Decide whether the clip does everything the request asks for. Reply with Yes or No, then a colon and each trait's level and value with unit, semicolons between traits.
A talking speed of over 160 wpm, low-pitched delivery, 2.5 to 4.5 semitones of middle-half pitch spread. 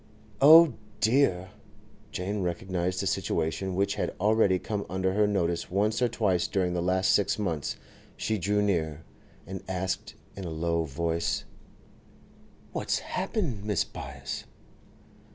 No: slow, 135 wpm; very low, 95 Hz; average, 2.9 semitones